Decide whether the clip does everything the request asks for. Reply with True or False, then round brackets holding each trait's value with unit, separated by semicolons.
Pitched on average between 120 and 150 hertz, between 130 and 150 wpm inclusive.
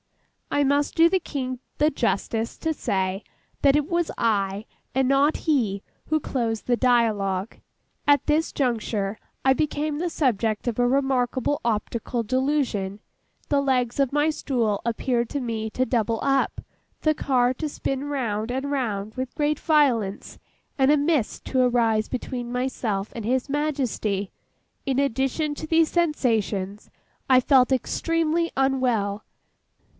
False (255 Hz; 145 wpm)